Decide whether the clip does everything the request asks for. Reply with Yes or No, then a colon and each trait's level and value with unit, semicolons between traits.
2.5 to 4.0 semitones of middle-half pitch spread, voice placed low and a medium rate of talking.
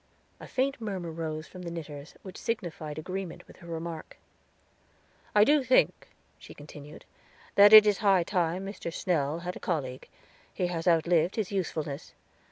No: average, 3.6 semitones; medium, 175 Hz; average, 160 wpm